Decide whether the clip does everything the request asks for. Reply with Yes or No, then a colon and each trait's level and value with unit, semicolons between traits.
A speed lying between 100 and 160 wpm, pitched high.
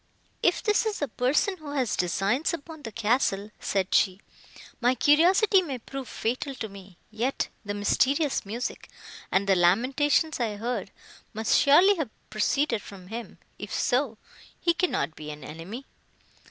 Yes: average, 155 wpm; high, 245 Hz